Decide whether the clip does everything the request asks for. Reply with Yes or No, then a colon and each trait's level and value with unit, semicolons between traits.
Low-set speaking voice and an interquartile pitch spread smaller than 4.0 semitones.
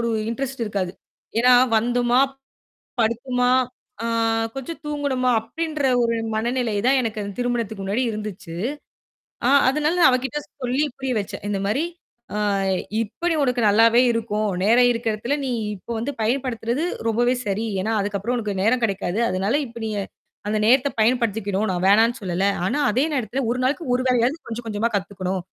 No: high, 235 Hz; average, 3.3 semitones